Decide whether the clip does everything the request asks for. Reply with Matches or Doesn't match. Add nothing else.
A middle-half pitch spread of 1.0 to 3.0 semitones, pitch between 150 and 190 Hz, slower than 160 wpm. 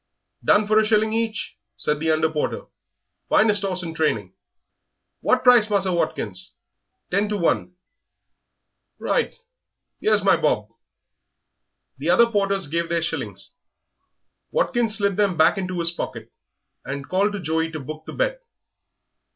Doesn't match